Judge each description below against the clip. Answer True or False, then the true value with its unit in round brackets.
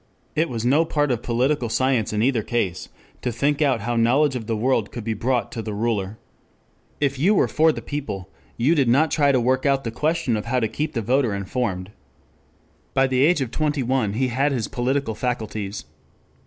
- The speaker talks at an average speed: False (210 wpm)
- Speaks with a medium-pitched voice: False (125 Hz)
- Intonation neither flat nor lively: True (3.9 semitones)